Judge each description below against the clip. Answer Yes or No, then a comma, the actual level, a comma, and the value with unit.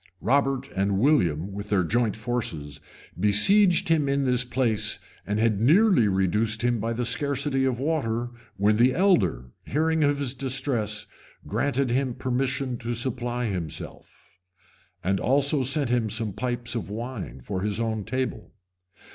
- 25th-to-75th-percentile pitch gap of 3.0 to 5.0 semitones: Yes, average, 4.5 semitones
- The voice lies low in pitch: Yes, low, 120 Hz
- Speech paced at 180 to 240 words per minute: No, average, 145 wpm